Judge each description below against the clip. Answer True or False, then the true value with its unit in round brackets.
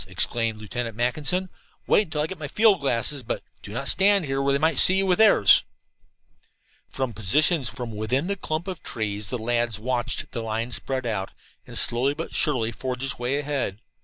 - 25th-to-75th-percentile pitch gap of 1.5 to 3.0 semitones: False (5.1 semitones)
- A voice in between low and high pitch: False (130 Hz)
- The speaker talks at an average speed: True (185 wpm)